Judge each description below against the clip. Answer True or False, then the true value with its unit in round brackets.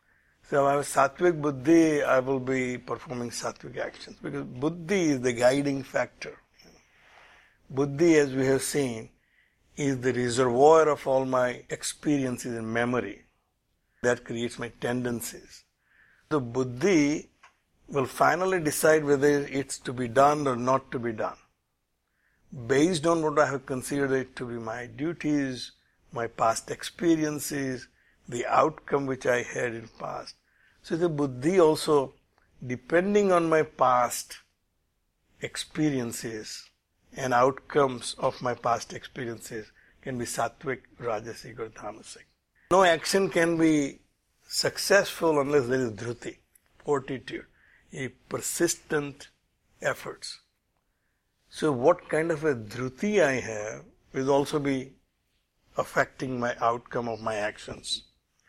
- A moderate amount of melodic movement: True (3.6 semitones)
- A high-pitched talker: False (135 Hz)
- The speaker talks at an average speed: False (125 wpm)